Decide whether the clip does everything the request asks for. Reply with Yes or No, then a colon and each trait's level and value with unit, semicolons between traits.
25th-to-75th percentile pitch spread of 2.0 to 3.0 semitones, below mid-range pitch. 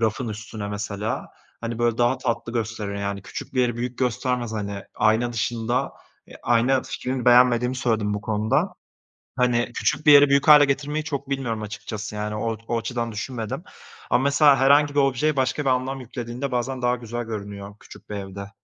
No: average, 3.5 semitones; low, 120 Hz